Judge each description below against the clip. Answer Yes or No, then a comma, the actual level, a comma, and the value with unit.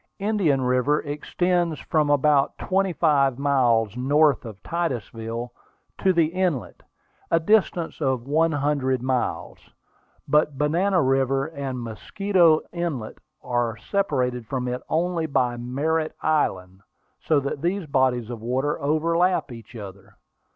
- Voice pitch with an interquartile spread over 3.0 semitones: Yes, average, 4.7 semitones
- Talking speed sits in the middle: No, slow, 125 wpm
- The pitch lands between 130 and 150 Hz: Yes, medium, 140 Hz